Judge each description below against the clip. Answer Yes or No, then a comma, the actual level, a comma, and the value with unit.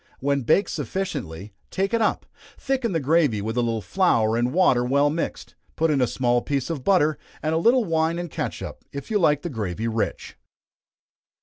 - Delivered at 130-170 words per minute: No, average, 190 wpm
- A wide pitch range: Yes, wide, 6.2 semitones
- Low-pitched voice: No, medium, 145 Hz